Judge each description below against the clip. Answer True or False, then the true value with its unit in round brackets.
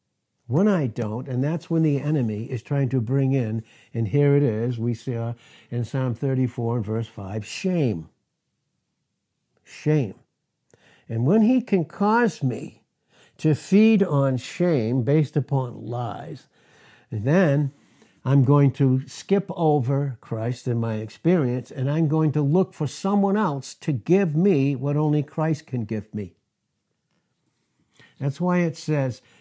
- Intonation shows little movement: False (4.6 semitones)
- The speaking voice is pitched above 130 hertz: True (140 Hz)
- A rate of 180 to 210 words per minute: False (145 wpm)